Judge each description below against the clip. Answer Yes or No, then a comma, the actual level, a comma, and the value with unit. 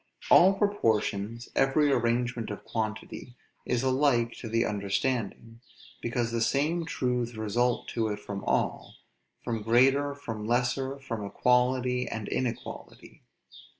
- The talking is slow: Yes, slow, 120 wpm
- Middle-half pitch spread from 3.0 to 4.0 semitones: No, narrow, 2.6 semitones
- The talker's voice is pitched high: No, low, 120 Hz